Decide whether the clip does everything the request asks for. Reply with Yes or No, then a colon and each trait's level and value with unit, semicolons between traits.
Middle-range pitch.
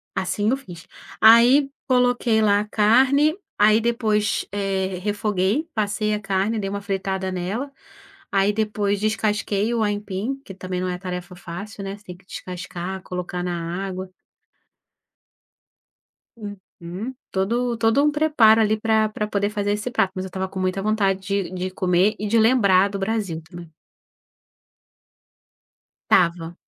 No: high, 205 Hz